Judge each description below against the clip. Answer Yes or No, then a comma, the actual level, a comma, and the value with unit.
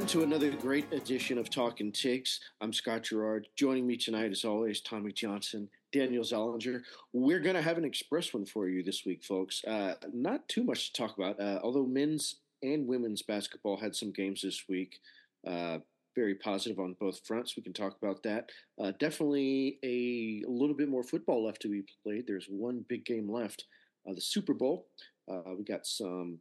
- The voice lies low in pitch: Yes, low, 110 Hz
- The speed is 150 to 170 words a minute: No, average, 195 wpm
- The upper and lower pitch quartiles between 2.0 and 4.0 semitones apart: No, average, 4.6 semitones